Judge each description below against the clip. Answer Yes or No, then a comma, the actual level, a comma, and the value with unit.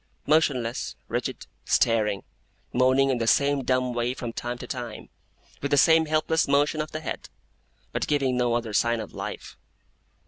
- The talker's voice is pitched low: Yes, low, 130 Hz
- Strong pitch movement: No, average, 3.3 semitones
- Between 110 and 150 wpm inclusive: No, average, 165 wpm